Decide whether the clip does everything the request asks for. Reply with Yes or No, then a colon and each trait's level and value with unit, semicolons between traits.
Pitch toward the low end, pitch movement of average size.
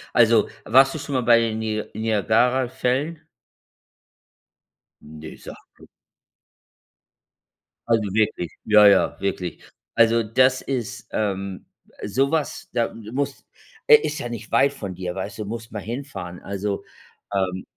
Yes: low, 110 Hz; average, 4.2 semitones